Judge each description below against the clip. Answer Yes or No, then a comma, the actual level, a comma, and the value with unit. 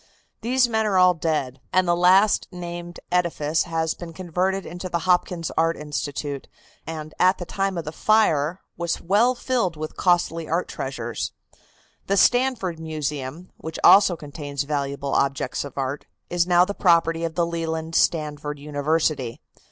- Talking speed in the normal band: Yes, average, 155 wpm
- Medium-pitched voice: Yes, medium, 165 Hz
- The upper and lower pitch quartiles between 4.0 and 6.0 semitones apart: No, average, 3.3 semitones